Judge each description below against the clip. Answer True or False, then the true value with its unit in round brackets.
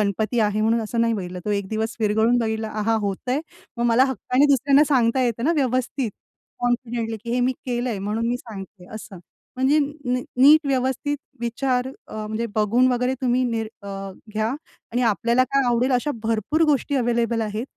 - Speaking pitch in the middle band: False (235 Hz)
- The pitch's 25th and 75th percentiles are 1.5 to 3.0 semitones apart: True (2.7 semitones)